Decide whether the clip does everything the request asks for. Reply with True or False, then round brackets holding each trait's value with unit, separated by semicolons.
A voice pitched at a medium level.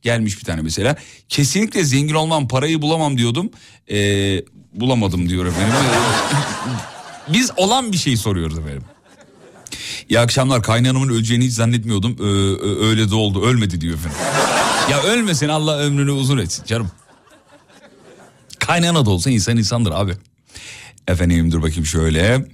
False (115 Hz)